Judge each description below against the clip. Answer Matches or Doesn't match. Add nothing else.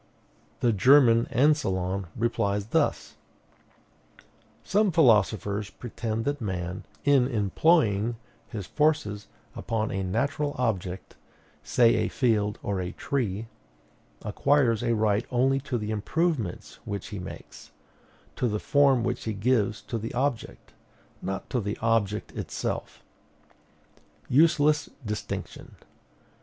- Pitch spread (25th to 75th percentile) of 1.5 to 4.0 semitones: Doesn't match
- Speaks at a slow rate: Matches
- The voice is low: Matches